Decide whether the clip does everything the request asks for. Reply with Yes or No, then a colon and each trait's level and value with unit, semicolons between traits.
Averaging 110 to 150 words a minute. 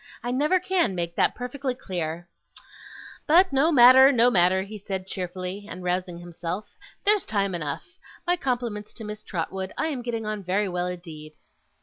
No: average, 165 wpm